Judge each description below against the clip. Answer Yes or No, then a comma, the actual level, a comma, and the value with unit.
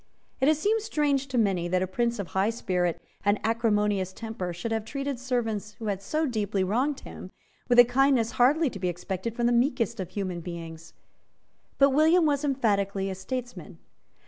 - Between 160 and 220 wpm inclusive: Yes, average, 185 wpm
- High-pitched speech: Yes, high, 225 Hz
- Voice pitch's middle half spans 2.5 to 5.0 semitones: No, wide, 5.5 semitones